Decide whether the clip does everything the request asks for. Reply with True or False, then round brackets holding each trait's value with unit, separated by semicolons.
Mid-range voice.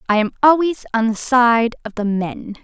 False (235 Hz)